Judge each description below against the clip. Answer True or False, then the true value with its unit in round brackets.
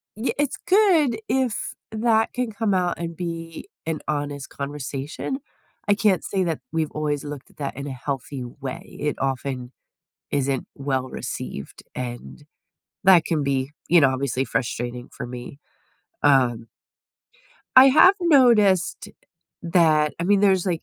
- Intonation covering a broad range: True (7.1 semitones)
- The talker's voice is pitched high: False (155 Hz)